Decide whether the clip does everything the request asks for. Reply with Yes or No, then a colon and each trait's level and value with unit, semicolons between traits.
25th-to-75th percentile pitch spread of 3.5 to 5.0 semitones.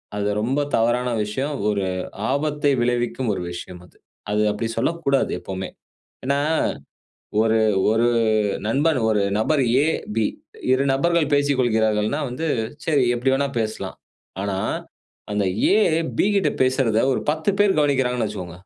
Yes: average, 4.7 semitones